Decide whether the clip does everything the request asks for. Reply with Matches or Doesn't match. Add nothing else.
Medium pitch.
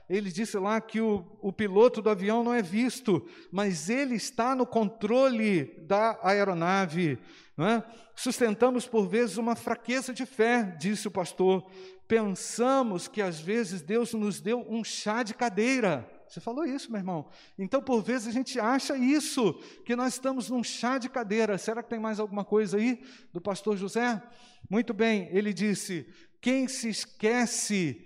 Doesn't match